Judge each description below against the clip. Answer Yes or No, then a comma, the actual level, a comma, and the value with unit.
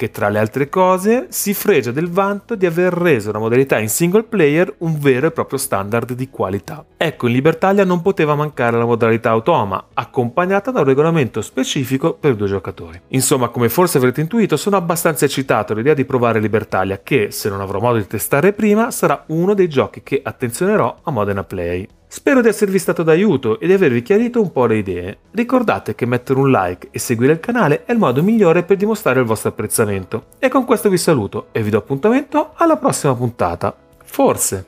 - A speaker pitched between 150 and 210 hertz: No, medium, 140 Hz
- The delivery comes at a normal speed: No, fast, 195 wpm